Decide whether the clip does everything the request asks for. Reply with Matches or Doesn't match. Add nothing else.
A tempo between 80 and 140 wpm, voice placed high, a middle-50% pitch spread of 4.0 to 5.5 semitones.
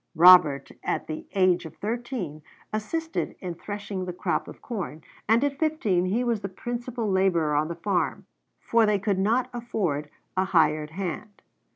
Doesn't match